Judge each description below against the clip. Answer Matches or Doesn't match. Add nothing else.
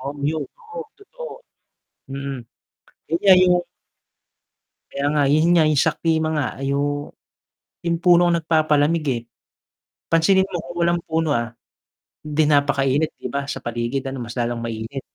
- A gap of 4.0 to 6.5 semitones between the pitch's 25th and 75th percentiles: Doesn't match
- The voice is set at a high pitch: Doesn't match